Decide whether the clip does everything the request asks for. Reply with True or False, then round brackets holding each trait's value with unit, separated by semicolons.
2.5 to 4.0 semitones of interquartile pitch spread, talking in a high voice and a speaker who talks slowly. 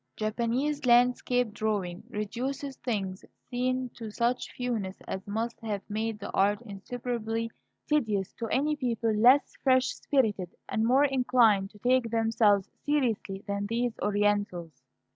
True (3.4 semitones; 225 Hz; 130 wpm)